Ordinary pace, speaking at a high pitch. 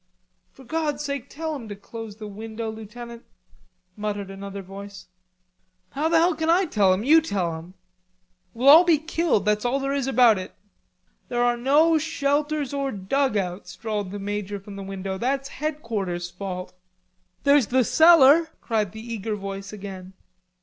Yes: average, 165 wpm; high, 230 Hz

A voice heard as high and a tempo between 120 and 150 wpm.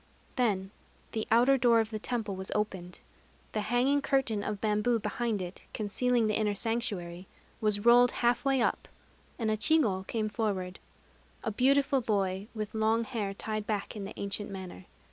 No: high, 215 Hz; average, 165 wpm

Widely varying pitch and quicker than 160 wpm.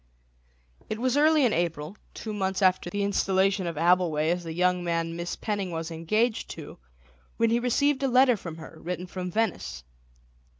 No: average, 4.8 semitones; average, 175 wpm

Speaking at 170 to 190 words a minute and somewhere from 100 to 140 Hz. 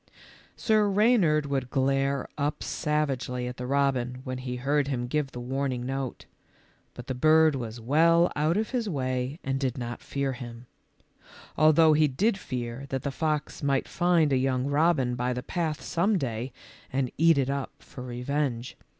Yes: average, 175 wpm; low, 135 Hz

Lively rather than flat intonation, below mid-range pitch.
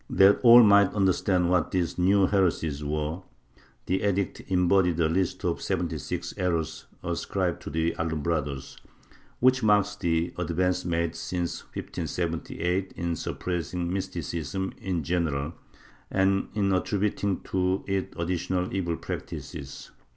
No: narrow, 2.6 semitones; very low, 90 Hz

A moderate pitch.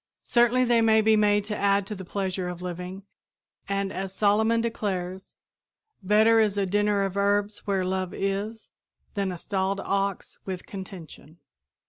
No: high, 200 Hz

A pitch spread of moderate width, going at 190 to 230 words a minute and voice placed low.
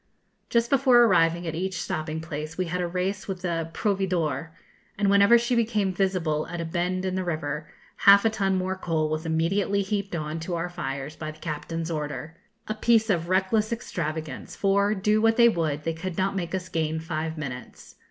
No: average, 3.7 semitones; average, 195 wpm; medium, 180 Hz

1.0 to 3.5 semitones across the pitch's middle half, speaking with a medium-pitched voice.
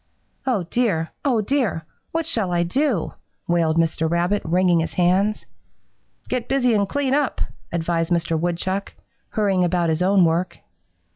No: average, 4.8 semitones; medium, 180 Hz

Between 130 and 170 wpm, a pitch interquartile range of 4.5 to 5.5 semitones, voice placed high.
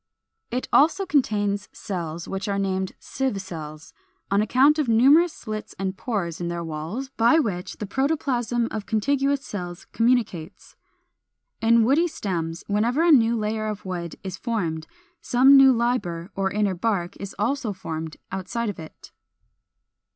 Yes: average, 150 wpm; average, 5.2 semitones; high, 210 Hz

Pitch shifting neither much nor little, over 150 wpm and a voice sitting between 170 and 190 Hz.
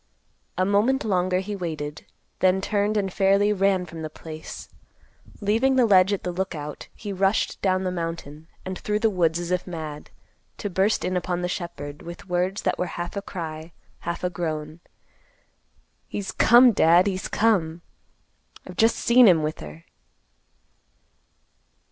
Yes: average, 3.3 semitones; average, 160 wpm; medium, 185 Hz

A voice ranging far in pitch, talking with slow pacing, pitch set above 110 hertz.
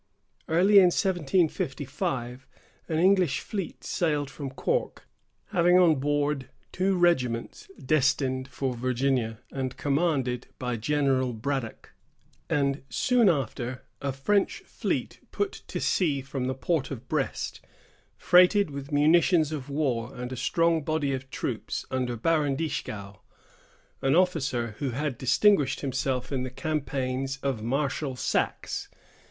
No: average, 3.9 semitones; slow, 125 wpm; medium, 140 Hz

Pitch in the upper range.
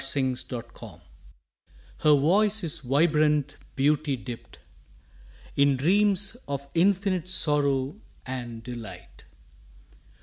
No: medium, 145 Hz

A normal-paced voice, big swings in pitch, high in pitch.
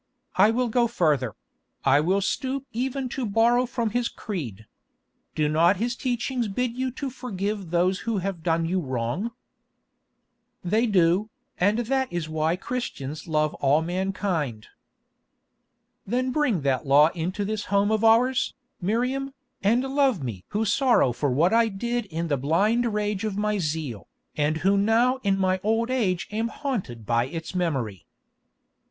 Yes: average, 155 wpm; wide, 6.7 semitones; high, 200 Hz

